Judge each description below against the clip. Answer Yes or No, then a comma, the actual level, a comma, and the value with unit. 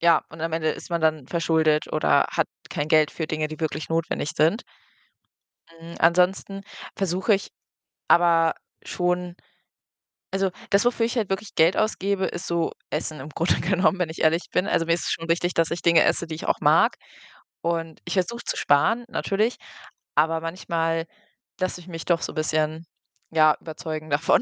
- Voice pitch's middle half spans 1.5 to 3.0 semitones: Yes, narrow, 2.4 semitones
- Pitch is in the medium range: Yes, medium, 165 Hz